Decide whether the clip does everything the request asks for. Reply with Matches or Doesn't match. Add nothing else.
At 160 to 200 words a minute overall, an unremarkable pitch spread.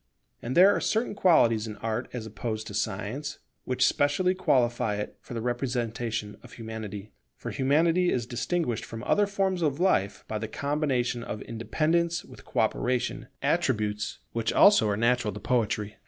Doesn't match